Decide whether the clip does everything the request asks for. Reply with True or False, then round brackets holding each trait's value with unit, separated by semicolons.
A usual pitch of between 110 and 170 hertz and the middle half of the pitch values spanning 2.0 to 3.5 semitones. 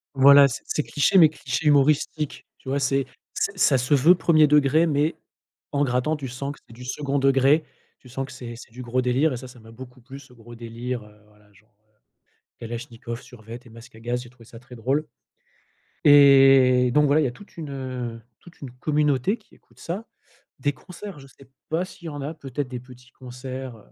True (130 Hz; 3.1 semitones)